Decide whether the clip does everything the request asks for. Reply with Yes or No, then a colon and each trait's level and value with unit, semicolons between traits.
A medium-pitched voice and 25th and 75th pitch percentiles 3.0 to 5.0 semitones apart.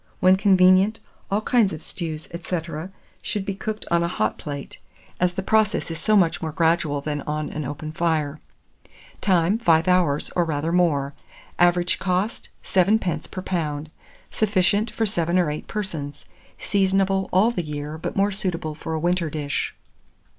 Yes: medium, 175 Hz; average, 3.8 semitones